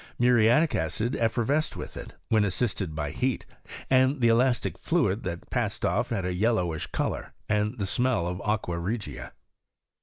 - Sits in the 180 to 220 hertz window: No, low, 110 Hz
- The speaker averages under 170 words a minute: Yes, average, 160 wpm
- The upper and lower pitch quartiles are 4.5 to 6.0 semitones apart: Yes, average, 5.1 semitones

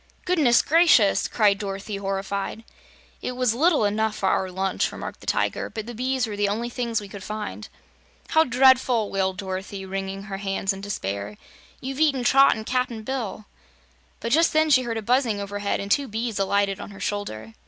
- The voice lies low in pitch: No, high, 215 Hz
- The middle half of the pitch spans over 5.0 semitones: No, average, 4.2 semitones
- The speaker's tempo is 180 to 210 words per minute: Yes, average, 185 wpm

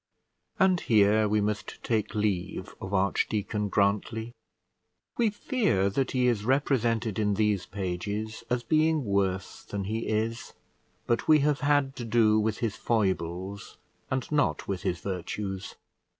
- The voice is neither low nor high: No, low, 110 Hz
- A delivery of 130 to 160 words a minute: Yes, average, 140 wpm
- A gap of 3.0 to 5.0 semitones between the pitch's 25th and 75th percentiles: Yes, average, 3.7 semitones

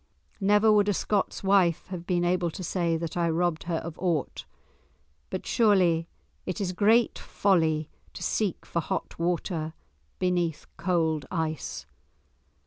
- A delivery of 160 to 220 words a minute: No, average, 140 wpm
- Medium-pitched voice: Yes, medium, 175 Hz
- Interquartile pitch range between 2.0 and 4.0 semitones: Yes, average, 2.8 semitones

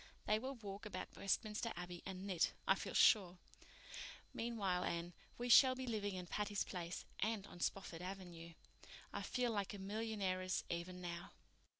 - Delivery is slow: No, average, 155 wpm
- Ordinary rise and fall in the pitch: Yes, average, 3.4 semitones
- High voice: Yes, high, 195 Hz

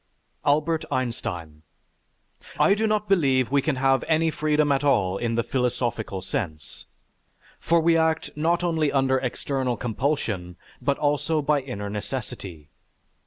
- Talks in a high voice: No, low, 135 Hz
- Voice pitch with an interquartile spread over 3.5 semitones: Yes, average, 5.0 semitones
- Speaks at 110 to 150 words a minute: Yes, slow, 135 wpm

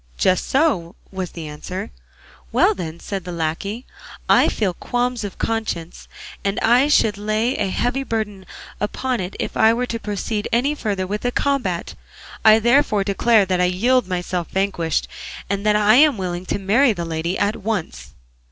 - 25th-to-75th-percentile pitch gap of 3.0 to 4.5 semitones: Yes, average, 4.2 semitones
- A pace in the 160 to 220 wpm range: Yes, average, 170 wpm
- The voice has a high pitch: Yes, high, 205 Hz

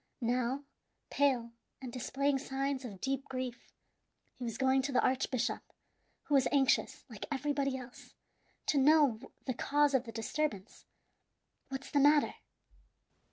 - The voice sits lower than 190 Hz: No, very high, 265 Hz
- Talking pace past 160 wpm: No, slow, 135 wpm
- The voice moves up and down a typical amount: No, narrow, 2.1 semitones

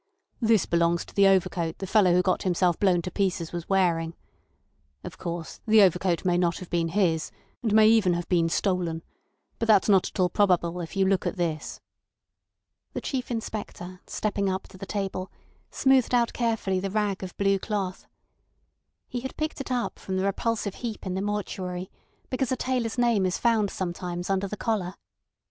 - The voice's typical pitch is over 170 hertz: Yes, high, 190 Hz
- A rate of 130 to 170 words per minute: No, average, 185 wpm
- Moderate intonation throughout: Yes, average, 3.3 semitones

